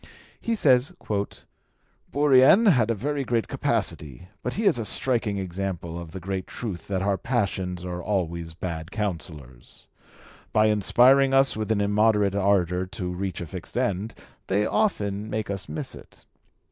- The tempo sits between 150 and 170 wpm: Yes, average, 155 wpm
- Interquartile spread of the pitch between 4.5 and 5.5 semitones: Yes, average, 4.8 semitones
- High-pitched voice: No, low, 100 Hz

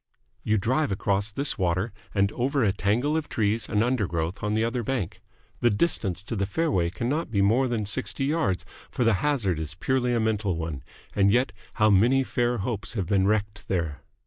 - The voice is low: Yes, low, 110 Hz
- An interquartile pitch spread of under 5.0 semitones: Yes, average, 4.1 semitones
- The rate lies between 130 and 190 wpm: No, average, 200 wpm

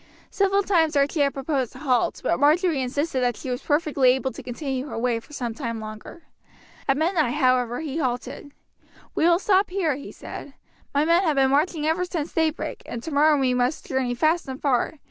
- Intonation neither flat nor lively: Yes, average, 4.0 semitones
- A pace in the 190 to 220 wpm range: Yes, average, 200 wpm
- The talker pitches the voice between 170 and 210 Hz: No, very high, 285 Hz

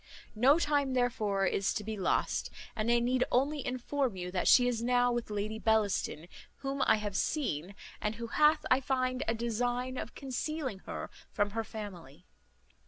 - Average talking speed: Yes, average, 170 wpm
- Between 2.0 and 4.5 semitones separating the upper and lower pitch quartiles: Yes, average, 3.6 semitones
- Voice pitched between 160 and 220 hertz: No, high, 235 Hz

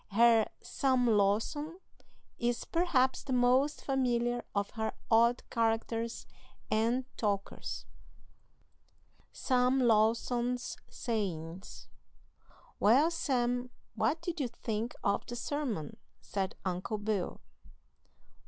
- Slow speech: Yes, slow, 95 wpm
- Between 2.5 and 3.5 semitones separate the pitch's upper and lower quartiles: Yes, average, 2.9 semitones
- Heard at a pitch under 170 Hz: No, high, 235 Hz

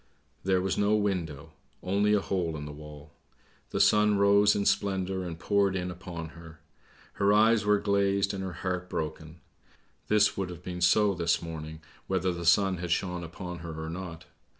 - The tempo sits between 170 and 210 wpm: Yes, average, 180 wpm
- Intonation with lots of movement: No, average, 3.2 semitones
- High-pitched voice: No, very low, 90 Hz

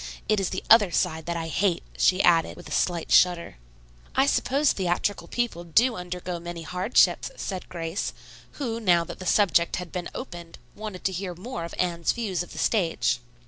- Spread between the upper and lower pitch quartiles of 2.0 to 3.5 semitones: Yes, average, 3.2 semitones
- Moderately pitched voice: Yes, medium, 180 Hz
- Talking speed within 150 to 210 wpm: Yes, average, 185 wpm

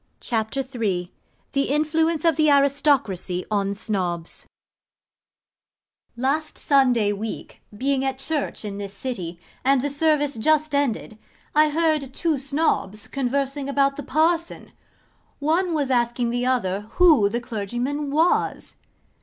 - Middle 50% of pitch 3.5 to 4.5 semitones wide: No, average, 5.3 semitones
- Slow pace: Yes, slow, 125 wpm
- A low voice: No, very high, 270 Hz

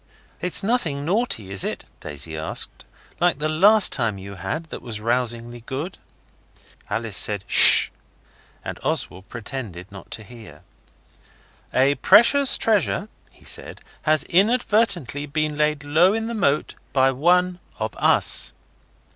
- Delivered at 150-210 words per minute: No, slow, 135 wpm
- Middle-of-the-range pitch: Yes, medium, 145 Hz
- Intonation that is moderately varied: No, wide, 7.9 semitones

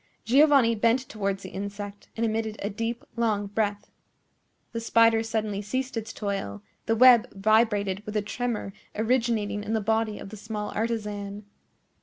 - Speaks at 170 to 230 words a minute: No, average, 155 wpm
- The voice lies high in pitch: Yes, high, 220 Hz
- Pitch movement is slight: Yes, narrow, 2.0 semitones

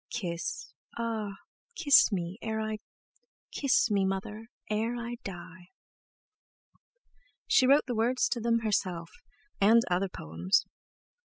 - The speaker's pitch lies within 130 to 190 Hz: No, high, 215 Hz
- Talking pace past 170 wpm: No, slow, 135 wpm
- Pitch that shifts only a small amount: No, average, 3.9 semitones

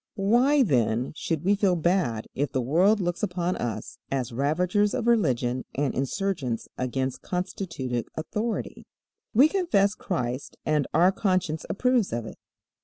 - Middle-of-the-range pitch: Yes, medium, 175 Hz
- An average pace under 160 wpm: Yes, average, 140 wpm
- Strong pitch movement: Yes, wide, 7.5 semitones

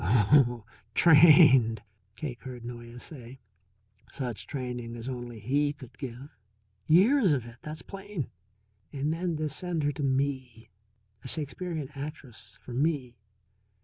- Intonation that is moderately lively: Yes, average, 4.0 semitones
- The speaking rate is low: Yes, slow, 130 wpm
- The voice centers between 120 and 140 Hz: Yes, low, 135 Hz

